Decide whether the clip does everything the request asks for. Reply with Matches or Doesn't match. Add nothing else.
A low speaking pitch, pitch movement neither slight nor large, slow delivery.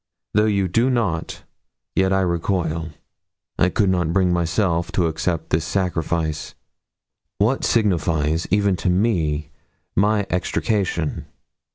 Matches